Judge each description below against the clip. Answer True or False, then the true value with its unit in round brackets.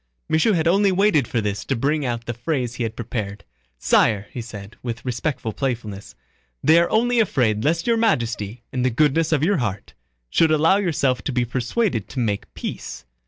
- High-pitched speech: False (125 Hz)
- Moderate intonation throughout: False (6.3 semitones)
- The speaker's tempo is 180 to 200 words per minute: True (190 wpm)